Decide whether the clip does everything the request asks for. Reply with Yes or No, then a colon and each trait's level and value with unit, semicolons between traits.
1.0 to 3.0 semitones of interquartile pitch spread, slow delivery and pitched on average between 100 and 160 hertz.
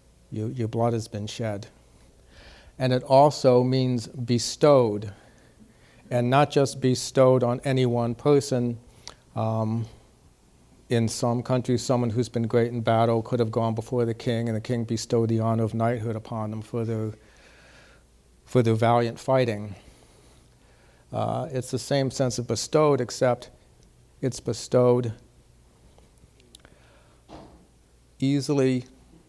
Yes: narrow, 2.4 semitones; slow, 125 wpm; low, 120 Hz